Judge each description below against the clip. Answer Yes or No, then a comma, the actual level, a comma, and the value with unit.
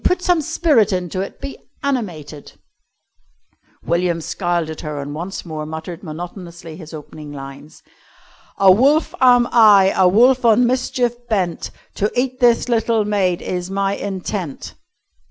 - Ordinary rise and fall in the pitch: No, wide, 6.3 semitones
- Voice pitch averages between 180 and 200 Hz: Yes, high, 190 Hz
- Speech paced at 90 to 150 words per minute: Yes, average, 140 wpm